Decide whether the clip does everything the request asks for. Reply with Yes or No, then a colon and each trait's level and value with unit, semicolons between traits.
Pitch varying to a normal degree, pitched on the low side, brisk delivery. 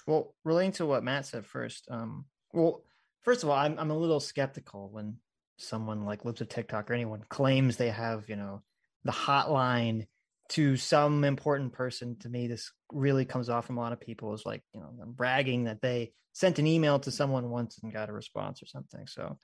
Yes: average, 3.7 semitones; low, 125 Hz; fast, 210 wpm